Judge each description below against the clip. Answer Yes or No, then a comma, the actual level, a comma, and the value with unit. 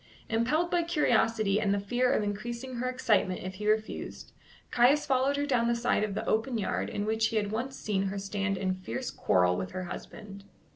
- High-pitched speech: Yes, high, 220 Hz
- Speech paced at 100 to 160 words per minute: No, fast, 205 wpm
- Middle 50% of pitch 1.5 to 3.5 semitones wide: No, average, 4.0 semitones